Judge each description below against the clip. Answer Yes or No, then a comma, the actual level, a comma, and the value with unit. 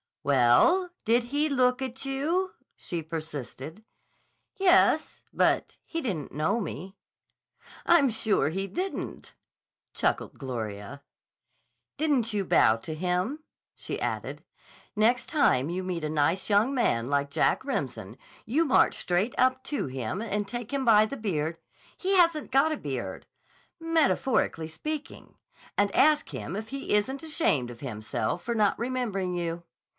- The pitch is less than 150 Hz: No, high, 210 Hz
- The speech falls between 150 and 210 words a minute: No, average, 140 wpm